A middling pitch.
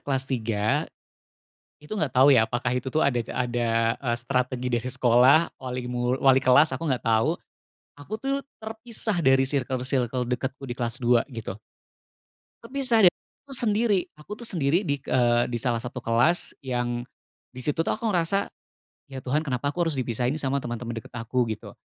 No: low, 130 Hz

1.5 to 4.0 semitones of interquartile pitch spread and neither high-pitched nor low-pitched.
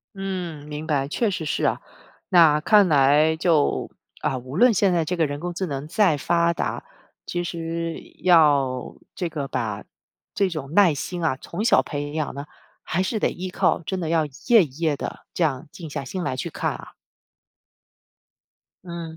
Yes: average, 3.5 semitones; medium, 160 Hz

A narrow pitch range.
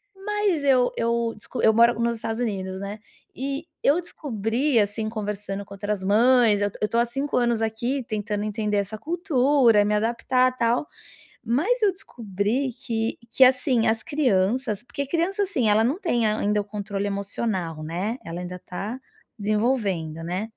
No: average, 4.0 semitones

